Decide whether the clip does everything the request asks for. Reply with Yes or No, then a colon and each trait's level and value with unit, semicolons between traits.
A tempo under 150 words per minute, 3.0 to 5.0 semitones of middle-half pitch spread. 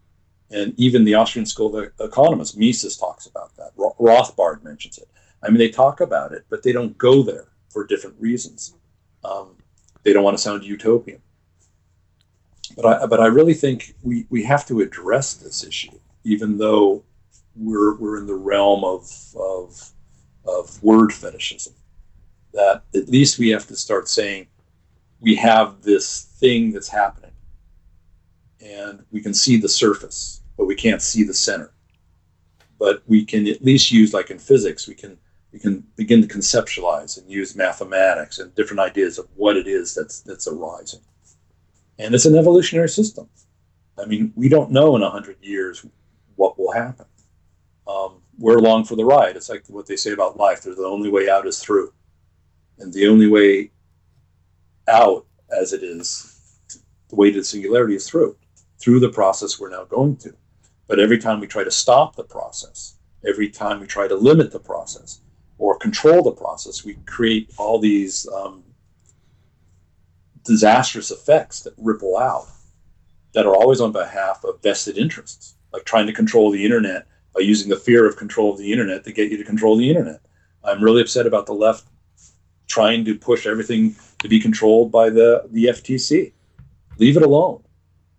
No: average, 175 wpm; average, 4.6 semitones